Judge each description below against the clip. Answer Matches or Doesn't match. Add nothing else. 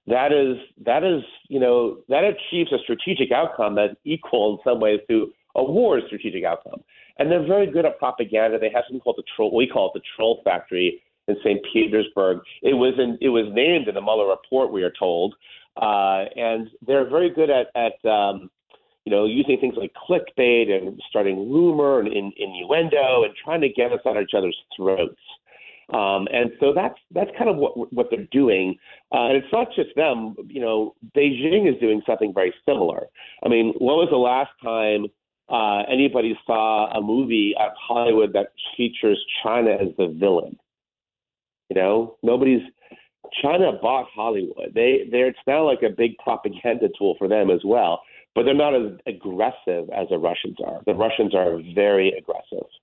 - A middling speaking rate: Matches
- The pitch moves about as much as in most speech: Doesn't match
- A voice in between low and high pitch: Doesn't match